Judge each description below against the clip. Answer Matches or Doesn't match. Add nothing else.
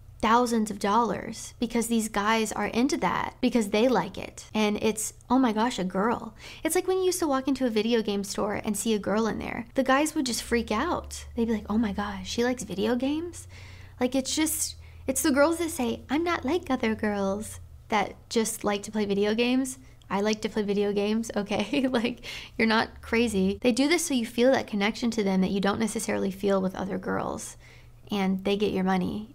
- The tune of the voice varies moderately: Matches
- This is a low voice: Doesn't match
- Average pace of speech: Doesn't match